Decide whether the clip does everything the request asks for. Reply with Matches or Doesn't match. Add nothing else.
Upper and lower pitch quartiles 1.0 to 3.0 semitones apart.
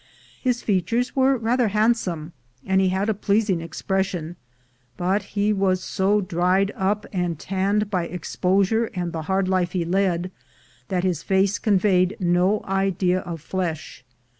Matches